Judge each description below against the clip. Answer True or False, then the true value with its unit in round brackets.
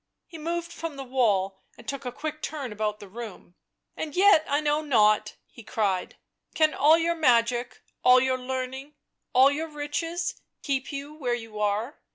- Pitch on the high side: True (265 Hz)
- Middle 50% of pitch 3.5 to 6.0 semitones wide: True (4.8 semitones)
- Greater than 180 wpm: True (190 wpm)